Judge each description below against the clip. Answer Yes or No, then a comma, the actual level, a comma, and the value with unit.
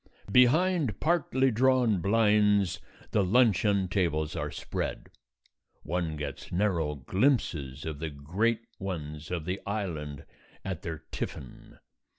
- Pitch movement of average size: No, wide, 6.3 semitones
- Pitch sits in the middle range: No, very low, 95 Hz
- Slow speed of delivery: Yes, slow, 115 wpm